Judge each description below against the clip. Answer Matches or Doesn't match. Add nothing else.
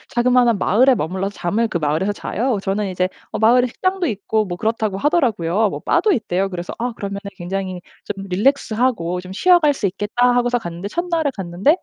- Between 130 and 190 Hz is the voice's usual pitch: Doesn't match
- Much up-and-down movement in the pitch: Doesn't match